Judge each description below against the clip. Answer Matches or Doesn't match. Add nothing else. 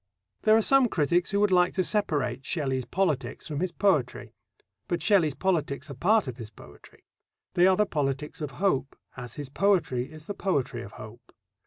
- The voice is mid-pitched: Matches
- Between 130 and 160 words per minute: Doesn't match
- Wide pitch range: Matches